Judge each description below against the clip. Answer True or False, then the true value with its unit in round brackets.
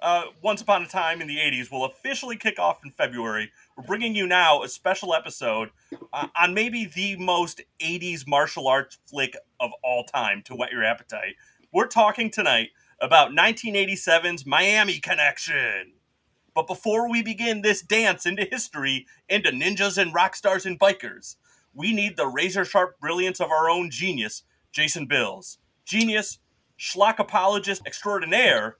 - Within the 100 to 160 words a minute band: True (155 wpm)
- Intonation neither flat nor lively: True (4.2 semitones)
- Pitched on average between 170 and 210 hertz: True (190 Hz)